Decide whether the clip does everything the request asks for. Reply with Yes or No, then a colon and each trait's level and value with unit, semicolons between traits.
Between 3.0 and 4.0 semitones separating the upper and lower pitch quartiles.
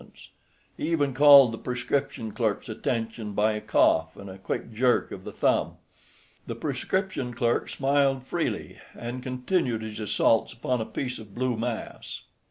Yes: average, 3.3 semitones